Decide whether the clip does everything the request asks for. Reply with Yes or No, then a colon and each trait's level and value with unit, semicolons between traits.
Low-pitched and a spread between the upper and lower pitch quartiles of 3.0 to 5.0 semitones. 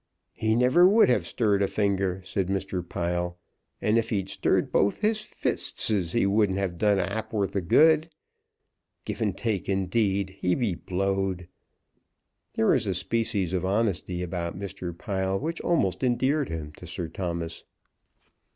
Yes: low, 100 Hz; average, 3.5 semitones